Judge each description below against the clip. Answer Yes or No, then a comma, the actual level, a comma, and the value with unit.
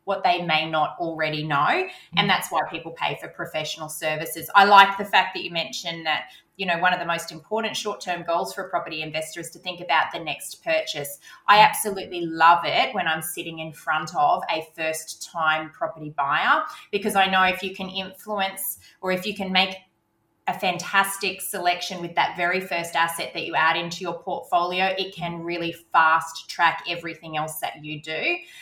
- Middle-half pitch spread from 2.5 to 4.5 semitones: Yes, average, 3.0 semitones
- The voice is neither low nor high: Yes, medium, 175 Hz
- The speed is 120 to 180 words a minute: No, average, 195 wpm